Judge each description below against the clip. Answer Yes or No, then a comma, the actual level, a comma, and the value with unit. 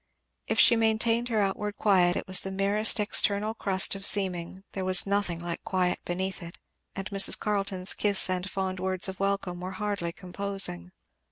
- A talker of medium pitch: No, high, 195 Hz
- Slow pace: No, average, 175 wpm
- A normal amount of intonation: No, narrow, 1.7 semitones